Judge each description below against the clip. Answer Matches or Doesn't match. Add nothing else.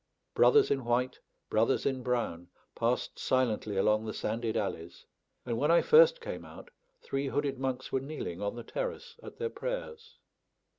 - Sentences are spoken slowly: Doesn't match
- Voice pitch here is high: Doesn't match